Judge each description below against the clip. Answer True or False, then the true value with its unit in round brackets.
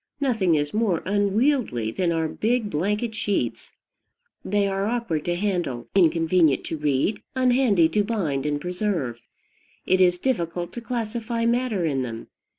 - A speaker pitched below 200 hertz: True (190 Hz)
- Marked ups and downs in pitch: True (5.7 semitones)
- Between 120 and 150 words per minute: True (145 wpm)